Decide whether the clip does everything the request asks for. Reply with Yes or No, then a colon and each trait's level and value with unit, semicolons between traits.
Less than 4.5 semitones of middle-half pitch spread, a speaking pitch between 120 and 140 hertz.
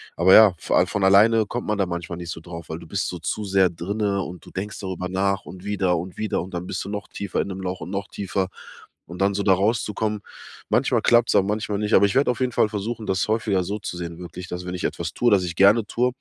No: average, 2.7 semitones; very low, 95 Hz